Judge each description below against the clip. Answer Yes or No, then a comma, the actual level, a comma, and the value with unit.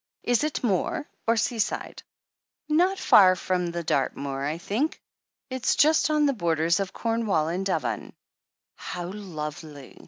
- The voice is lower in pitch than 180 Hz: No, high, 190 Hz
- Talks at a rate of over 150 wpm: No, slow, 135 wpm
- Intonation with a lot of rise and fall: Yes, wide, 6.9 semitones